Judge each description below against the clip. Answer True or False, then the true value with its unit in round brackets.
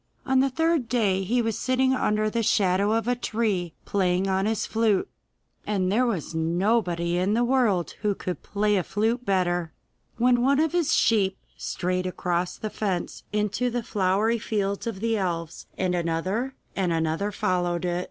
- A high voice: True (205 Hz)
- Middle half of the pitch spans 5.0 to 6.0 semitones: False (4.1 semitones)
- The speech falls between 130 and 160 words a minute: False (170 wpm)